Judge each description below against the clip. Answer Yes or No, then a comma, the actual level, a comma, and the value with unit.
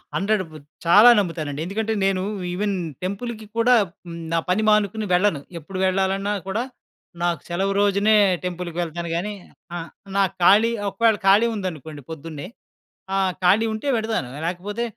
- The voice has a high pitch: Yes, high, 195 Hz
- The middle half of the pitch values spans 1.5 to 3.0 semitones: No, average, 3.7 semitones